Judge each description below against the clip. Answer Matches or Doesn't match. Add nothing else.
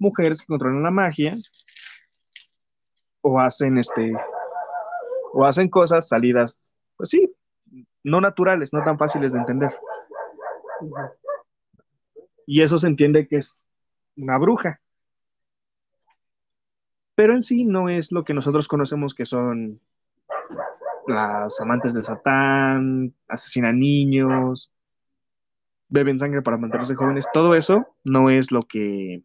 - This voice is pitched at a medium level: Matches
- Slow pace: Matches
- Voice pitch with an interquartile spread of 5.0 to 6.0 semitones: Matches